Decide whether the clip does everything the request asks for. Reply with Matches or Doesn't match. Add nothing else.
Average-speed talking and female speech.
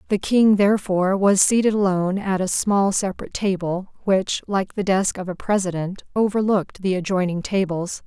Matches